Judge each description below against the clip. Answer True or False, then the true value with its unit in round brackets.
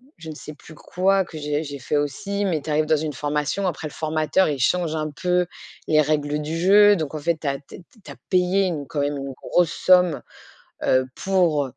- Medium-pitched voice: True (155 Hz)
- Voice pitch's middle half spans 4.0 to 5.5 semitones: False (3.5 semitones)